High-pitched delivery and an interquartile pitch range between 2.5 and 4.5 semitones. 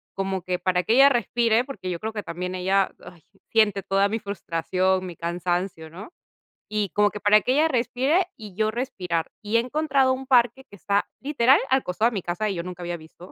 No: high, 205 Hz; average, 5.0 semitones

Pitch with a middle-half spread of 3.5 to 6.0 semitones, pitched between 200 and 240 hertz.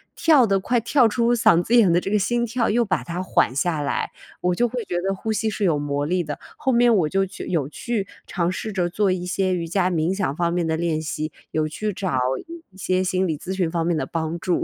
No: average, 4.1 semitones; medium, 185 Hz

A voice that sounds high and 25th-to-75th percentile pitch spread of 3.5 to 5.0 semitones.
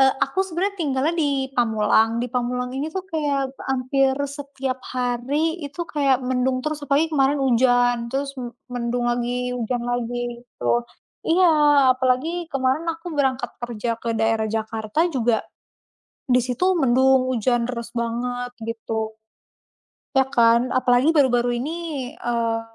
No: very high, 255 Hz; average, 2.8 semitones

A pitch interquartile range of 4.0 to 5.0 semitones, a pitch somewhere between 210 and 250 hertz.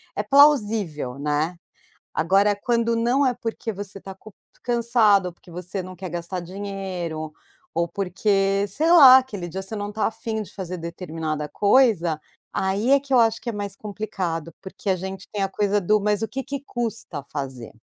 No: average, 4.3 semitones; high, 195 Hz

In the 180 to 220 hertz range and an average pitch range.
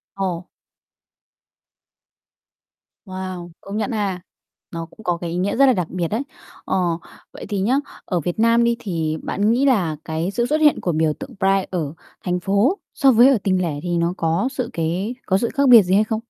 Yes: high, 190 Hz; average, 5.0 semitones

